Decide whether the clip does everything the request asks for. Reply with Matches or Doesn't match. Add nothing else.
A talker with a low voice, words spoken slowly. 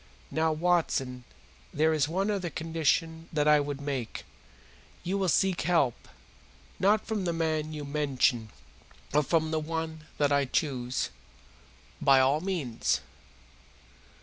Doesn't match